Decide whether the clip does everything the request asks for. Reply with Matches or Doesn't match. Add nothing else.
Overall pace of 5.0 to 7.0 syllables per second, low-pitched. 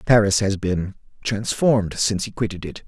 Matches